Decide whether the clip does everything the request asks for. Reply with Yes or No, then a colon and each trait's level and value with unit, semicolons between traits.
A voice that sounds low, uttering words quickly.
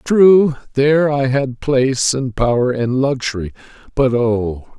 No: low, 130 Hz; average, 140 wpm